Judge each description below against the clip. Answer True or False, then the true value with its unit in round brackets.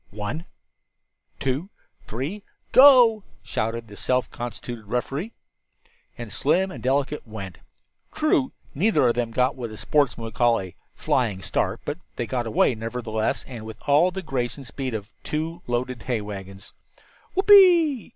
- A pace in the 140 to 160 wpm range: True (145 wpm)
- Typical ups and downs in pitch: False (6.6 semitones)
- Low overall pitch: True (125 Hz)